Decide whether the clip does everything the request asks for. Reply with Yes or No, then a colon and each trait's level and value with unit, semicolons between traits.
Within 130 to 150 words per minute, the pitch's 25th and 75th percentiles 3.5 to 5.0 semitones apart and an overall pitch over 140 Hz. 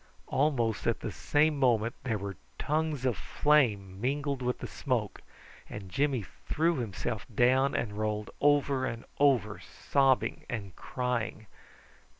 No: slow, 135 wpm; average, 4.6 semitones; low, 125 Hz